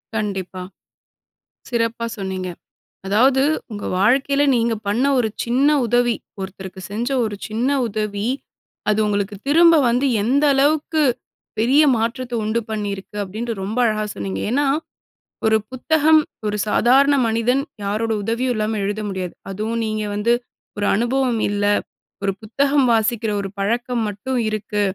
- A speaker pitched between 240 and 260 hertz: No, high, 225 Hz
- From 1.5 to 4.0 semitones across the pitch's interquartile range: Yes, average, 3.4 semitones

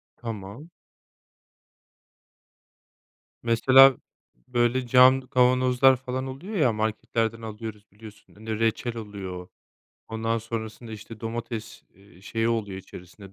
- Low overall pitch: Yes, low, 115 Hz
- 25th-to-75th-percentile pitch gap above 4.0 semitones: No, average, 2.8 semitones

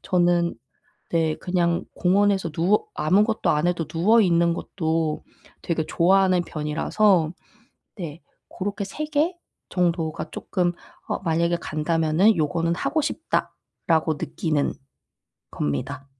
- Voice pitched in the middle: Yes, medium, 170 Hz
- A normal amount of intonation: Yes, average, 3.3 semitones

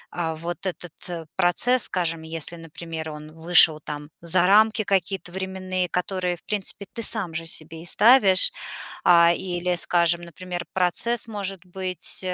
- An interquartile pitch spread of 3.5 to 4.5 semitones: No, narrow, 2.4 semitones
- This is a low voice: No, medium, 175 Hz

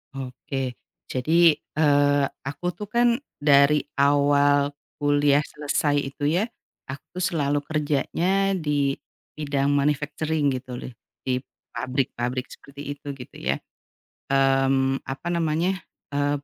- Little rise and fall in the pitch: Yes, narrow, 1.5 semitones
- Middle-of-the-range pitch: Yes, medium, 145 Hz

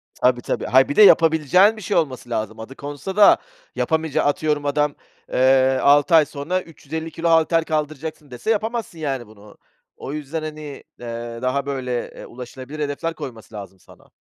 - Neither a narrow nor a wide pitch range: Yes, average, 4.0 semitones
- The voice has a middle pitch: Yes, medium, 145 Hz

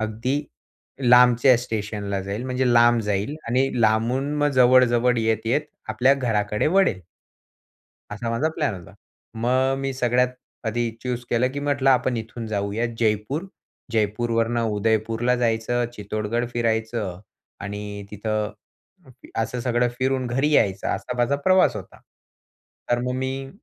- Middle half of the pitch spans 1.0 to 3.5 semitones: Yes, average, 2.8 semitones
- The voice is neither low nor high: No, low, 120 Hz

